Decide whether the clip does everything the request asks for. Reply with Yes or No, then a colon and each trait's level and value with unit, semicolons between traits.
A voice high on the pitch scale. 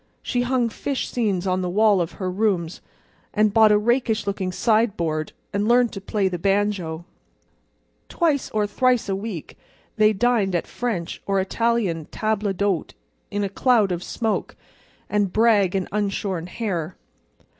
Yes: high, 205 Hz